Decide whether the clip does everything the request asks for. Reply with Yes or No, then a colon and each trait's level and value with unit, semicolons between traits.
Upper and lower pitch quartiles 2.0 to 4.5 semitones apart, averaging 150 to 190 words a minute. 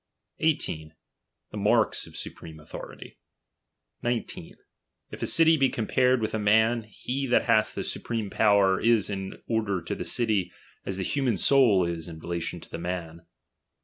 No: average, 5.2 semitones; average, 160 wpm